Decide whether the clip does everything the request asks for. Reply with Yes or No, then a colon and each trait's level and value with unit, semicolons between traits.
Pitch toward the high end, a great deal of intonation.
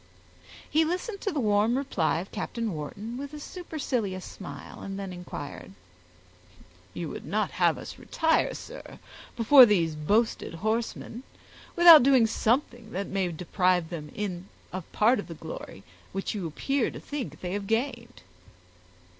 Yes: high, 215 Hz; wide, 6.3 semitones